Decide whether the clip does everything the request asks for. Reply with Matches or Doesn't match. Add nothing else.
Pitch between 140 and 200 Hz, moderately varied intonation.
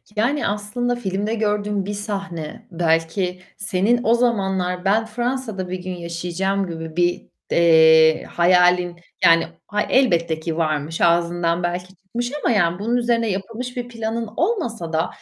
Matches